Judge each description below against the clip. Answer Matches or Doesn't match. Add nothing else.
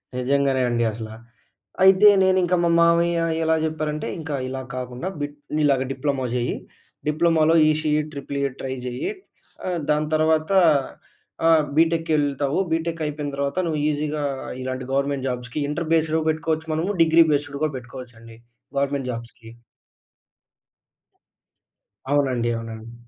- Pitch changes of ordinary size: Matches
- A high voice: Doesn't match